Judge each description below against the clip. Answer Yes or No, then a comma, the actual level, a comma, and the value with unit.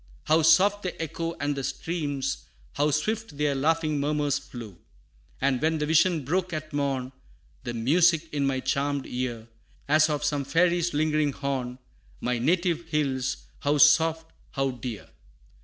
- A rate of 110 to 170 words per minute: Yes, average, 150 wpm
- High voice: No, medium, 150 Hz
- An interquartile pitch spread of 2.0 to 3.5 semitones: Yes, average, 3.1 semitones